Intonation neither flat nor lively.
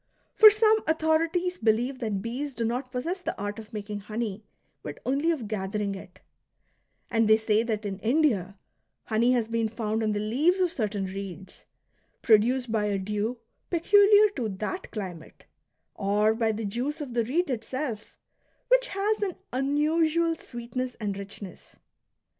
No: wide, 6.4 semitones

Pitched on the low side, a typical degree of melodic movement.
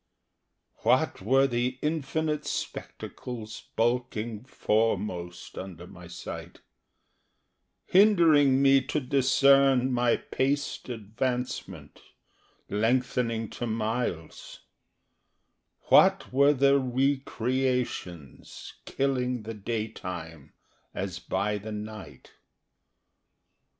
Yes: low, 120 Hz; average, 4.1 semitones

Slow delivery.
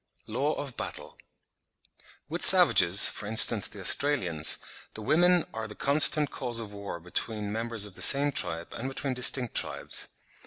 No: average, 160 wpm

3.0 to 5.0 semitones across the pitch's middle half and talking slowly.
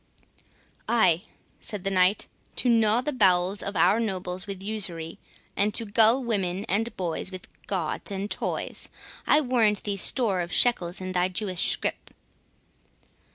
No: average, 3.4 semitones; average, 145 wpm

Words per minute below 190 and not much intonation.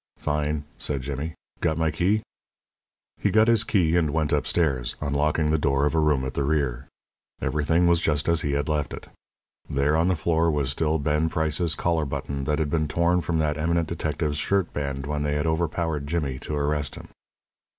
No: average, 195 wpm; narrow, 2.1 semitones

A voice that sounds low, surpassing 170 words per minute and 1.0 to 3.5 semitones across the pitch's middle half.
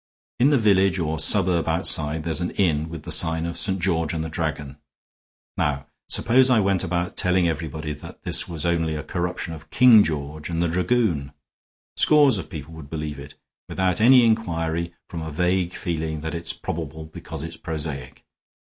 Yes: very low, 85 Hz; average, 180 wpm; average, 2.9 semitones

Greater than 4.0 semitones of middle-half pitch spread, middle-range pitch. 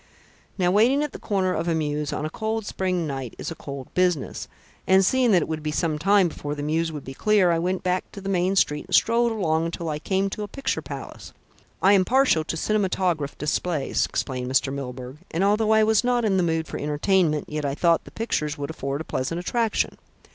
Yes: average, 5.0 semitones; medium, 175 Hz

